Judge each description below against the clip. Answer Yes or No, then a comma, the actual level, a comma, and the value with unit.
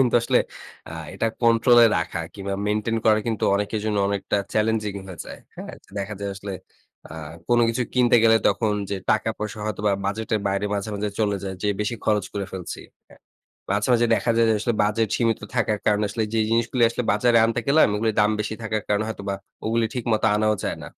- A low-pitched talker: Yes, low, 110 Hz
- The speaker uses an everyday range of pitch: No, narrow, 2.0 semitones